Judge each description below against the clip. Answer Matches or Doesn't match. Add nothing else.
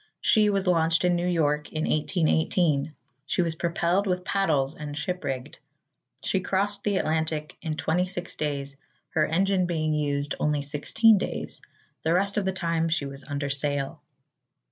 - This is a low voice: Doesn't match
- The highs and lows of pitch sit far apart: Doesn't match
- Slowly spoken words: Doesn't match